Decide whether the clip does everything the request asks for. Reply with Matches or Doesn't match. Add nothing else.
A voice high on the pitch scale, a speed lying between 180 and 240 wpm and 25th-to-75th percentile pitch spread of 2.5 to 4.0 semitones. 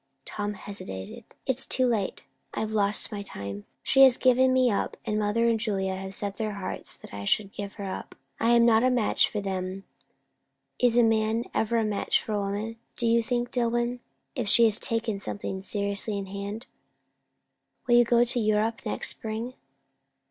Matches